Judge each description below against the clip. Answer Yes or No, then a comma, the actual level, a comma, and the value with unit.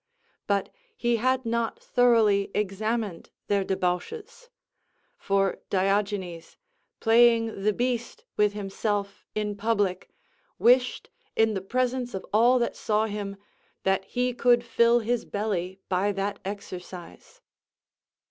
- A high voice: Yes, high, 210 Hz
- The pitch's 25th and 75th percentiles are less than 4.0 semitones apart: Yes, average, 3.4 semitones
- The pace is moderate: No, slow, 115 wpm